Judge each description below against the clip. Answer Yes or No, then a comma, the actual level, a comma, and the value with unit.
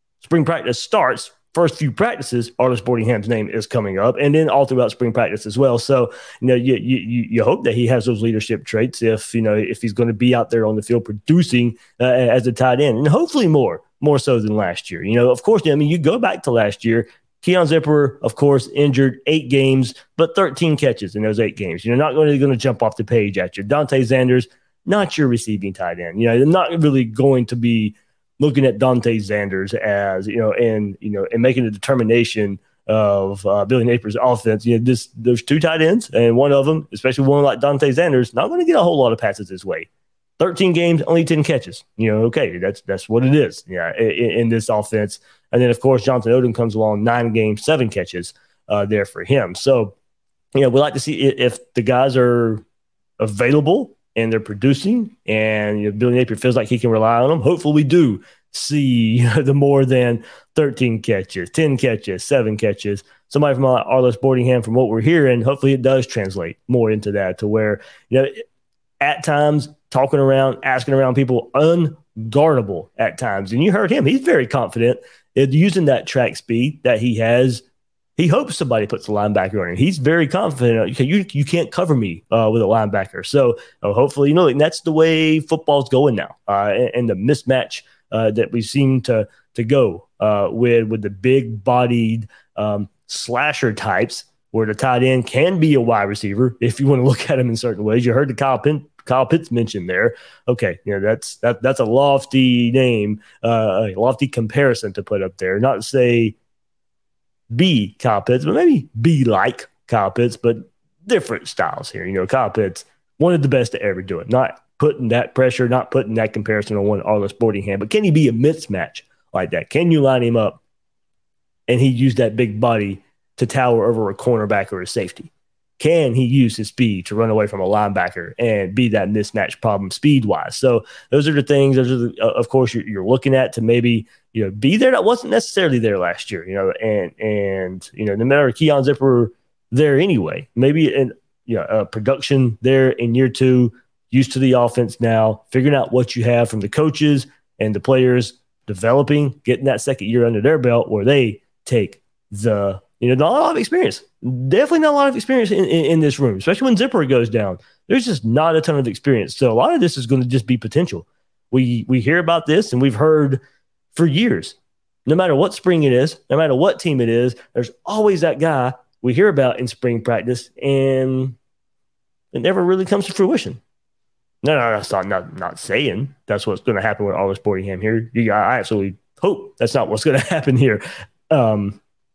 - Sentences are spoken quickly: Yes, fast, 215 wpm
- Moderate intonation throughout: Yes, average, 3.9 semitones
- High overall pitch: No, low, 125 Hz